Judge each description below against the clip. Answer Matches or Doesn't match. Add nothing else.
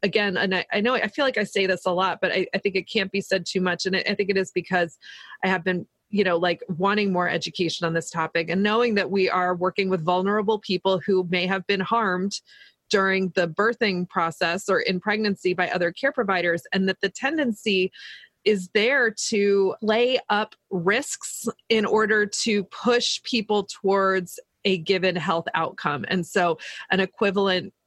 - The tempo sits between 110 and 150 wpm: Doesn't match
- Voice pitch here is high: Matches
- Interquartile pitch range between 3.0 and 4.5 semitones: Doesn't match